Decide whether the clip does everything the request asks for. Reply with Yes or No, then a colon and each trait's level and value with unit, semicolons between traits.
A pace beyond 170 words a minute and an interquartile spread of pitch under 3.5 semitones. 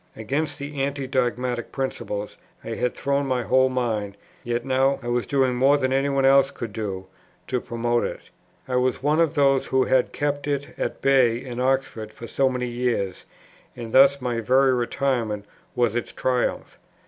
Yes: average, 180 wpm; narrow, 2.4 semitones